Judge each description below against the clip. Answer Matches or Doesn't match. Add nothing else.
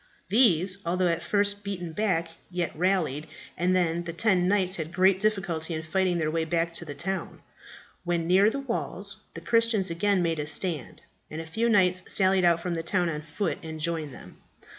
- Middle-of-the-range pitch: Matches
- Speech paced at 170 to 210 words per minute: Matches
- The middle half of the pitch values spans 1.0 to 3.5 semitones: Matches